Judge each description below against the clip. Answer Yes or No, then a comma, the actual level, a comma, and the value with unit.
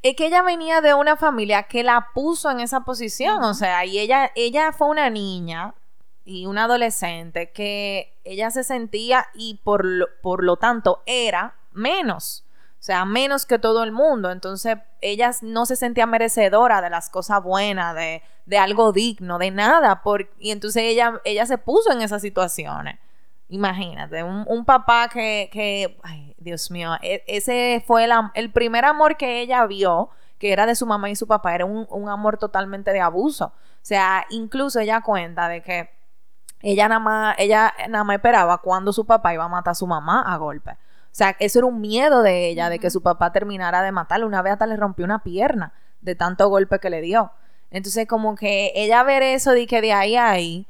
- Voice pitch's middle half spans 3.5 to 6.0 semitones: Yes, average, 4.2 semitones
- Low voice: No, high, 210 Hz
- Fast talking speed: Yes, fast, 200 wpm